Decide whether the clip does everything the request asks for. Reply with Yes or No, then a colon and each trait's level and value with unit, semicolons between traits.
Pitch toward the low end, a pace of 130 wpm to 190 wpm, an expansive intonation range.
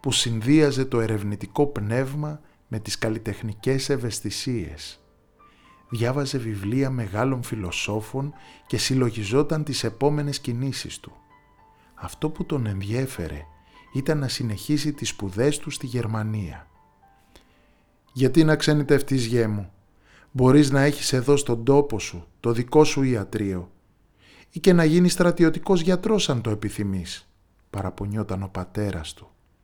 No: low, 120 Hz; average, 120 wpm; wide, 6.2 semitones